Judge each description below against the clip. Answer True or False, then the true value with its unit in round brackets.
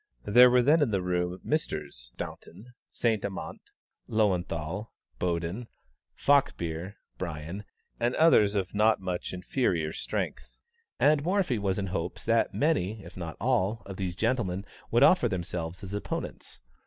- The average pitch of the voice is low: True (100 Hz)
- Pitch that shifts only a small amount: False (4.7 semitones)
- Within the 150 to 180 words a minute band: False (140 wpm)